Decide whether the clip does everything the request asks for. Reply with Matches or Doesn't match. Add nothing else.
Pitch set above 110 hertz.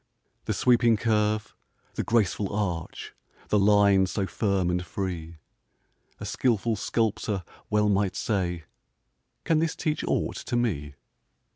Doesn't match